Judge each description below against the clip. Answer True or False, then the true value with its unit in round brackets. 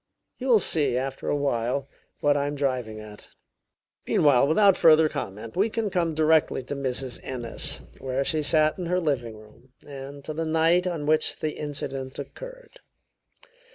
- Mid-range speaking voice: True (145 Hz)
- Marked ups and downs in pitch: False (3.6 semitones)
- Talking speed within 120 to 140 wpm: False (165 wpm)